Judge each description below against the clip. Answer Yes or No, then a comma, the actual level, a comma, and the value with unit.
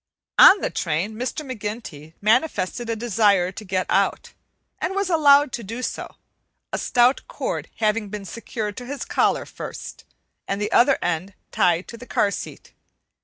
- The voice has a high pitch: Yes, high, 220 Hz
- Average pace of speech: Yes, average, 165 wpm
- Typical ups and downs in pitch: Yes, average, 4.3 semitones